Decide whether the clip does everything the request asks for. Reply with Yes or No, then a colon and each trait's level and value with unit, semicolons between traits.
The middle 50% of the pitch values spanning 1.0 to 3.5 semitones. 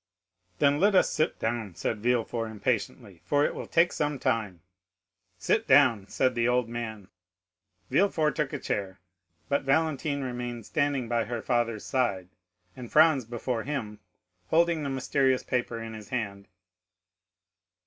No: average, 4.3 semitones